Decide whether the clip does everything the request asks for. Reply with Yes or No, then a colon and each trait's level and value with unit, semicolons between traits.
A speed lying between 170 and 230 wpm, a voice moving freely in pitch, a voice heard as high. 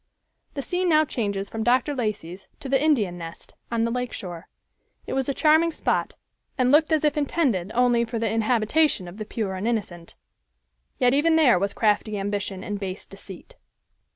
Yes: average, 180 wpm; wide, 5.8 semitones; high, 230 Hz